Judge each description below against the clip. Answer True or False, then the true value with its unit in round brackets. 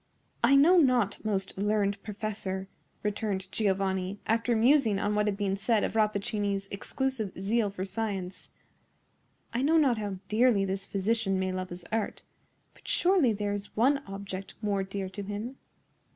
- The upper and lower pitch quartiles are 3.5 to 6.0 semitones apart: False (2.6 semitones)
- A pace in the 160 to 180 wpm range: False (150 wpm)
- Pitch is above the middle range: True (205 Hz)